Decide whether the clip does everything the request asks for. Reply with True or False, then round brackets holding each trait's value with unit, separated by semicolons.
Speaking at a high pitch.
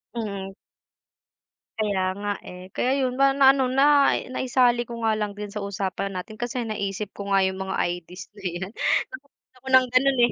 True (215 Hz)